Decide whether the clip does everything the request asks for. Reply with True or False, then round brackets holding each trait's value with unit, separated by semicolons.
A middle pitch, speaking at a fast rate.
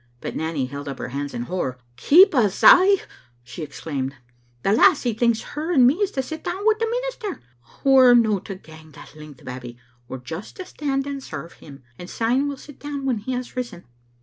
False (225 Hz; 225 wpm)